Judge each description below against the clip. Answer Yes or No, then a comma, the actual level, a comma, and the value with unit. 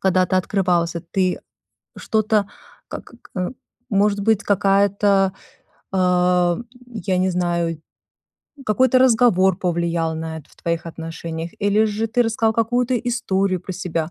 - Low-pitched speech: No, high, 190 Hz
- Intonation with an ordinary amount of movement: Yes, average, 3.7 semitones